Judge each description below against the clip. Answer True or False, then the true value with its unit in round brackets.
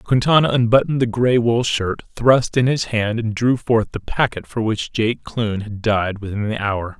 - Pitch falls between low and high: False (115 Hz)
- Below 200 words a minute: False (205 wpm)